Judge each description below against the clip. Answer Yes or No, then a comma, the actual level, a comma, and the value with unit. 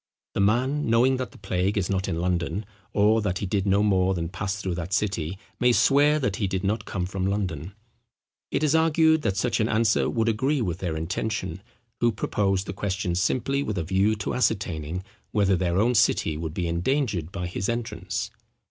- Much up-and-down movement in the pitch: No, average, 4.0 semitones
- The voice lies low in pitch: Yes, low, 100 Hz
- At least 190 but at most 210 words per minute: Yes, average, 200 wpm